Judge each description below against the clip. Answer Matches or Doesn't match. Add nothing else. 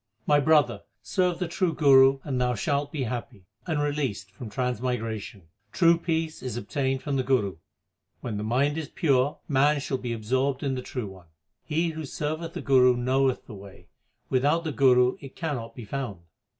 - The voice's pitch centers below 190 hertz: Matches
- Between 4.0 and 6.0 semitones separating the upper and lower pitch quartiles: Doesn't match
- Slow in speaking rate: Doesn't match